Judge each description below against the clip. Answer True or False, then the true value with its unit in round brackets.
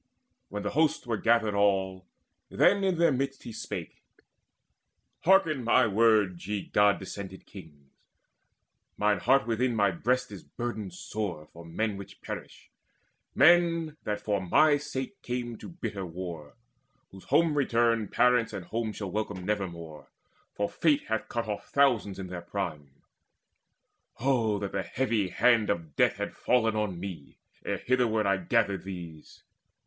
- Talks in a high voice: False (105 Hz)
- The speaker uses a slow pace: False (150 wpm)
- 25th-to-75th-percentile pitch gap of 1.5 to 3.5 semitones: False (4.6 semitones)